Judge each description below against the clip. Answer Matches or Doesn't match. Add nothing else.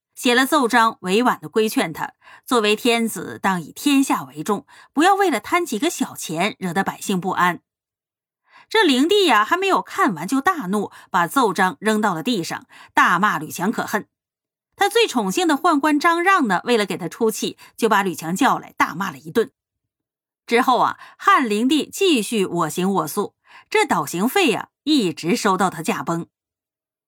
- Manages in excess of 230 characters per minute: Matches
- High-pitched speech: Matches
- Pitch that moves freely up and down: Matches